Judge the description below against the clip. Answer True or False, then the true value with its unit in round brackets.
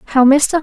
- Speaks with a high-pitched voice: True (280 Hz)